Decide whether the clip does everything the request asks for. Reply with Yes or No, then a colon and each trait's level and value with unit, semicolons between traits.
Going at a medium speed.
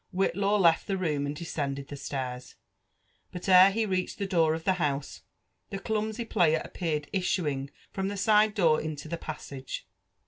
Yes: average, 170 wpm